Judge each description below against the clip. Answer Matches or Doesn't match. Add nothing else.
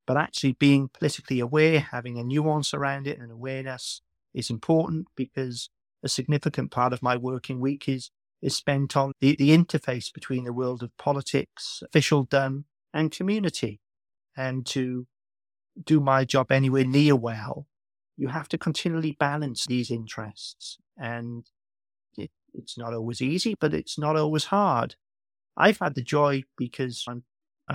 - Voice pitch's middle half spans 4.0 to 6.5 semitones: Doesn't match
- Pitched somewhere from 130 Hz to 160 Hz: Matches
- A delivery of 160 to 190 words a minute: Doesn't match